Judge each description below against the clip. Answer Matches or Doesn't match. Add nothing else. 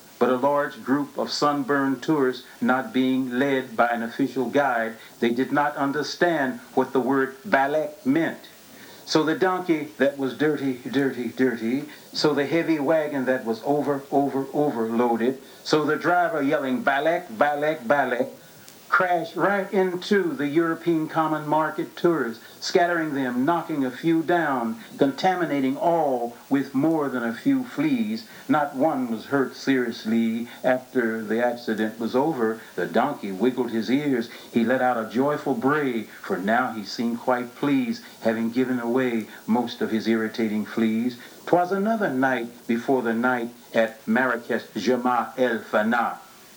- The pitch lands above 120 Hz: Matches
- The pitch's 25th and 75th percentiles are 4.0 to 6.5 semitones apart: Matches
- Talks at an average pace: Matches